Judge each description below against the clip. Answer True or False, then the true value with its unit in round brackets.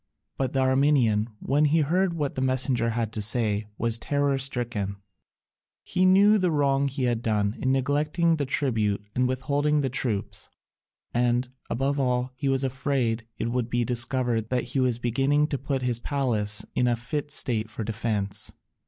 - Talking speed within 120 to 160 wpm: False (170 wpm)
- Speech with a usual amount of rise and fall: True (3.3 semitones)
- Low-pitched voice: True (130 Hz)